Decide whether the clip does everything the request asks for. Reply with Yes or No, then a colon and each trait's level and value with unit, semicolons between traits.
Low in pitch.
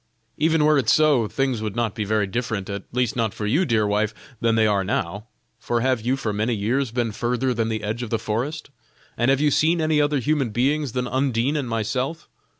Yes: low, 120 Hz